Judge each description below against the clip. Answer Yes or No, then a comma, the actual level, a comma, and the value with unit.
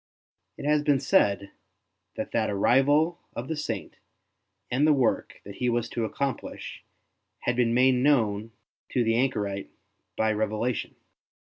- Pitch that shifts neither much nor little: Yes, average, 4.1 semitones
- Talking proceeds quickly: No, average, 140 wpm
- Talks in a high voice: No, low, 125 Hz